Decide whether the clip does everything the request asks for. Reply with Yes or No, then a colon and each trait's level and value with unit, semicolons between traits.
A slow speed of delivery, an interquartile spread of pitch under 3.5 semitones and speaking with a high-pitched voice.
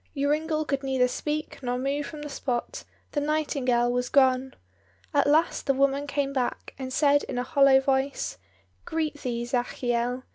No: average, 160 wpm; average, 2.7 semitones; very high, 275 Hz